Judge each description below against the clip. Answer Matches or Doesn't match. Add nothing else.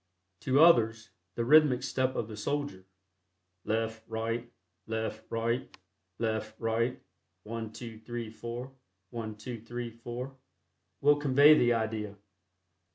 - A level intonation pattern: Matches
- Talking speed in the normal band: Doesn't match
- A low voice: Matches